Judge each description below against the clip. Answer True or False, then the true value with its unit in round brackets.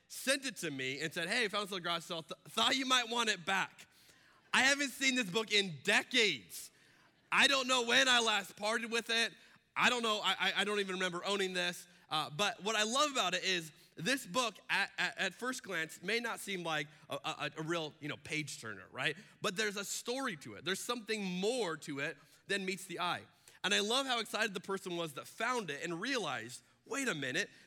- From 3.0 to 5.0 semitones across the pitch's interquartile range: False (5.6 semitones)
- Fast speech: True (220 wpm)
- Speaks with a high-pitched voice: True (195 Hz)